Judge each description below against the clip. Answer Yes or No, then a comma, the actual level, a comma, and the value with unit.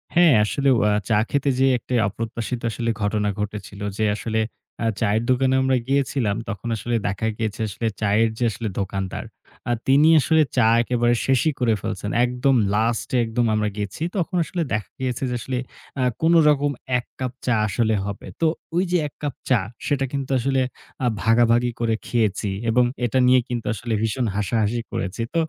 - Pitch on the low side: Yes, low, 120 Hz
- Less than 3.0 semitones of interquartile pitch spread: No, average, 3.6 semitones